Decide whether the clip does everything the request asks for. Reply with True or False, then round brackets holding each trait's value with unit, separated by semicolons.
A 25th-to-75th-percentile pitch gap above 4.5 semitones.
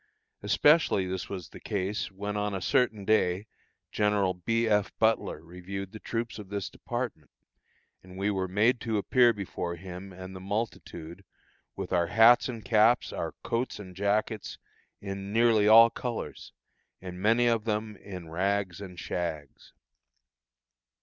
False (3.3 semitones)